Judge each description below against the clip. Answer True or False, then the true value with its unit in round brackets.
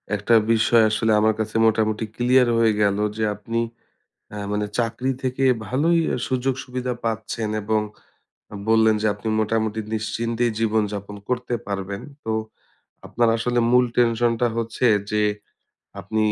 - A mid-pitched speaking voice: False (110 Hz)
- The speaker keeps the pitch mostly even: True (2.2 semitones)